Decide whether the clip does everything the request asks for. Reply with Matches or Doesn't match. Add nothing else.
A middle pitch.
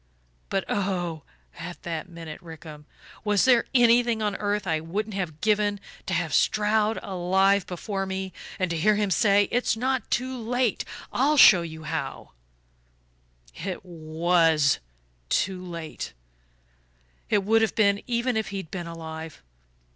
Doesn't match